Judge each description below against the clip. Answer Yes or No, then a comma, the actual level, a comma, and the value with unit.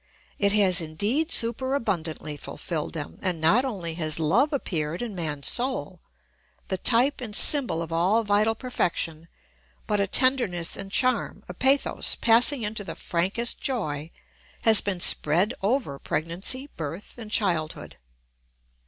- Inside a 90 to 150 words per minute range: Yes, average, 140 wpm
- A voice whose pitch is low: No, high, 200 Hz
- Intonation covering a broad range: Yes, wide, 6.5 semitones